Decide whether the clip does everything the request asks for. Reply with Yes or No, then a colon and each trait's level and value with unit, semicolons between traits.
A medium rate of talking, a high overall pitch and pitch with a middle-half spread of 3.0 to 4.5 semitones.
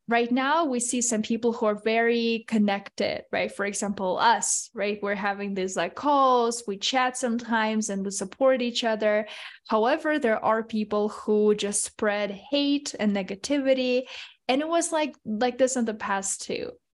Yes: average, 170 wpm; high, 225 Hz; average, 3.8 semitones